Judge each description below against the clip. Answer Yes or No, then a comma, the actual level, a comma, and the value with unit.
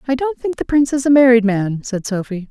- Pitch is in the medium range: No, high, 235 Hz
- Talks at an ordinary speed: No, fast, 265 wpm